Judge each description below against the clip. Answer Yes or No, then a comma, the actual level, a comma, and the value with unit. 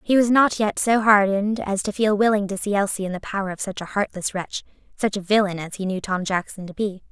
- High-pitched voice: Yes, high, 200 Hz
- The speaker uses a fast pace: Yes, fast, 260 wpm